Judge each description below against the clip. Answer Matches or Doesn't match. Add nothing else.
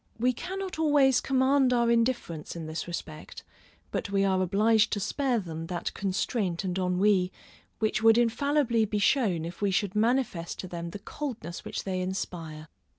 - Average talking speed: Matches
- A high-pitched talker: Matches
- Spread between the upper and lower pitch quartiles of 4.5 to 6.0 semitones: Matches